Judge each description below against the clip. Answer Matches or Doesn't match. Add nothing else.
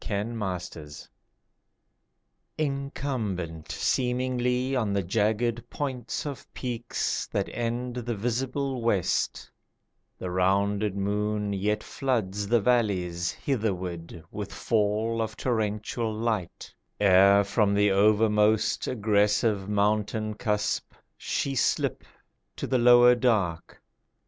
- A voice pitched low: Matches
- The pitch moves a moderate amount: Matches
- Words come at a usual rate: Doesn't match